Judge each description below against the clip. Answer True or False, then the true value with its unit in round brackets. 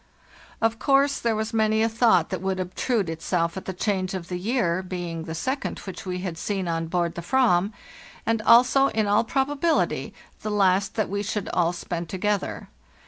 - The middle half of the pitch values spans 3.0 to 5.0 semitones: True (4.1 semitones)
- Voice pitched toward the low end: False (195 Hz)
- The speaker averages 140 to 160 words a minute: False (190 wpm)